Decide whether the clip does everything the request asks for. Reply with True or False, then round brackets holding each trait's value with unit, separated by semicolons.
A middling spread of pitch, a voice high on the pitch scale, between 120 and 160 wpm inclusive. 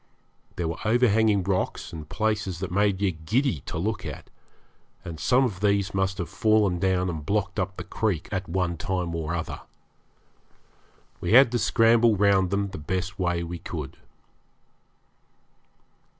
False (3.3 semitones; 95 Hz; 155 wpm)